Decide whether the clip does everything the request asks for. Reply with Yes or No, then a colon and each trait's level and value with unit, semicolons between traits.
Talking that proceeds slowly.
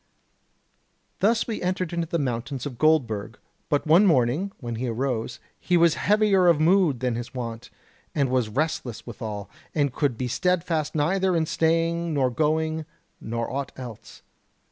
No: average, 155 wpm